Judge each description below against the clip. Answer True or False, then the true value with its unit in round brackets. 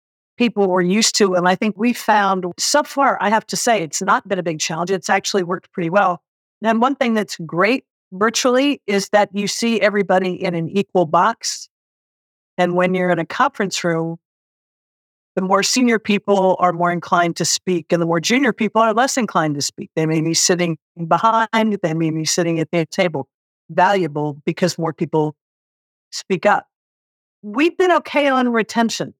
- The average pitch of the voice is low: False (190 Hz)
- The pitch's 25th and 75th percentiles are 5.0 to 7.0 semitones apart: False (4.3 semitones)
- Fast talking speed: False (185 wpm)